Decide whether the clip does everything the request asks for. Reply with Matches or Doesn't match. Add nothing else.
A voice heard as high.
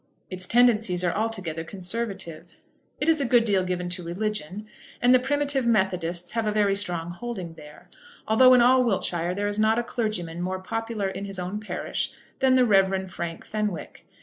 Matches